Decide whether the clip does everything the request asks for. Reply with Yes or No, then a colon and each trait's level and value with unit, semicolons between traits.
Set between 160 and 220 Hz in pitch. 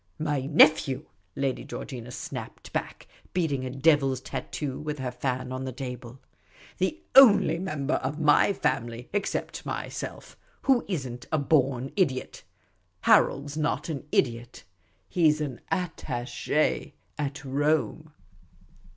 No: medium, 140 Hz